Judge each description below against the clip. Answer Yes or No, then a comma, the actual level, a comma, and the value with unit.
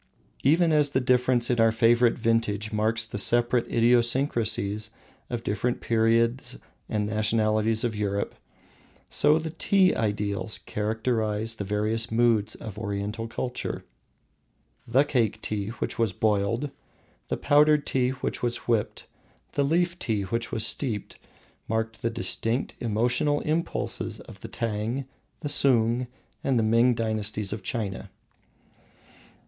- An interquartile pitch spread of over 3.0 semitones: No, narrow, 2.6 semitones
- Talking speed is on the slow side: Yes, slow, 130 wpm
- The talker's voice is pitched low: Yes, low, 115 Hz